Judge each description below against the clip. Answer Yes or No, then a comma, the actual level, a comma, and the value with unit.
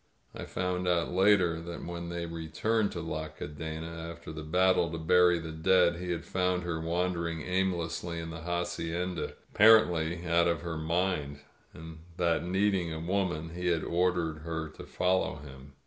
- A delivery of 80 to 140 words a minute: No, average, 175 wpm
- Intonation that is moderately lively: No, narrow, 1.8 semitones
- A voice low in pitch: Yes, very low, 85 Hz